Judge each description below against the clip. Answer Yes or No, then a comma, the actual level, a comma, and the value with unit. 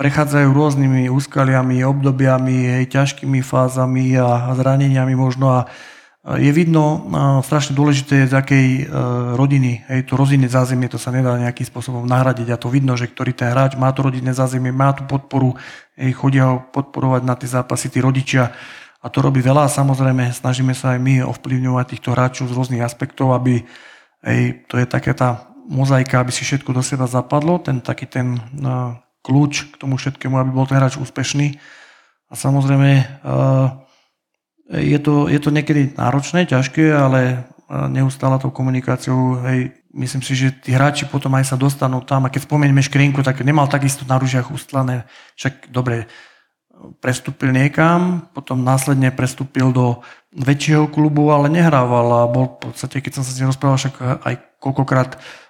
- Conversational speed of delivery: No, fast, 170 wpm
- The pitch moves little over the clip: Yes, narrow, 1.5 semitones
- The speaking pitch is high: No, low, 130 Hz